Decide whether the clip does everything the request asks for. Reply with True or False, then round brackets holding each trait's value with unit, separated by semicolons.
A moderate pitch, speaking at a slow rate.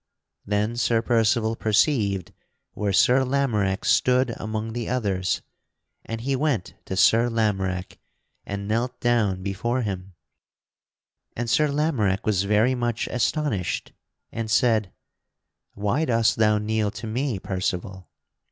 False (110 Hz; 125 wpm)